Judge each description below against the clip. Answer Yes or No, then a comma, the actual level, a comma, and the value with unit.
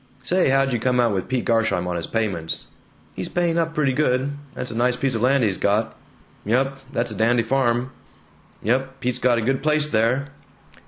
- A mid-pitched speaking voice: No, low, 125 Hz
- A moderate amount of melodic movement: Yes, average, 3.1 semitones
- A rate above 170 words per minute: Yes, average, 200 wpm